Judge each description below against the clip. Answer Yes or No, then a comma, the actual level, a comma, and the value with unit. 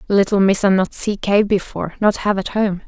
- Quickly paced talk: Yes, fast, 210 wpm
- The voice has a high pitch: Yes, high, 200 Hz